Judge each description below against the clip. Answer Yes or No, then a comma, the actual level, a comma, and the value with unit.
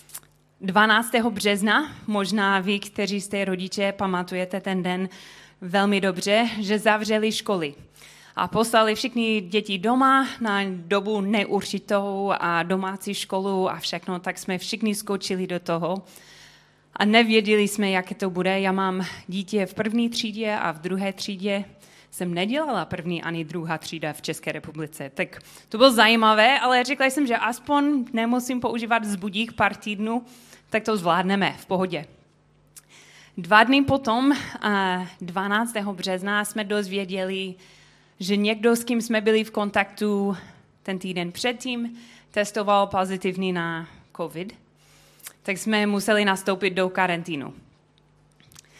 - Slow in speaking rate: No, average, 130 wpm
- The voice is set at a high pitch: Yes, high, 200 Hz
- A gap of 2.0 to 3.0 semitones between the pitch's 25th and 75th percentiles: Yes, average, 2.7 semitones